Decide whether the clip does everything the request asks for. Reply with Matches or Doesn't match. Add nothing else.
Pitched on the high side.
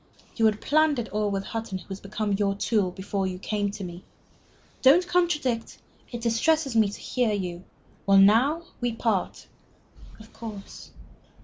Matches